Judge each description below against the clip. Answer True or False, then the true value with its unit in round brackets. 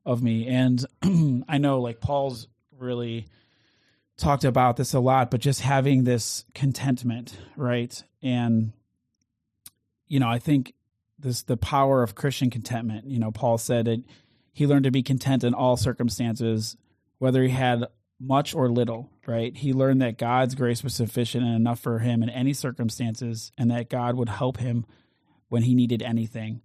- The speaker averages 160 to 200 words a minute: True (165 wpm)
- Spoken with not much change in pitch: True (2.1 semitones)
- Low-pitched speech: True (120 Hz)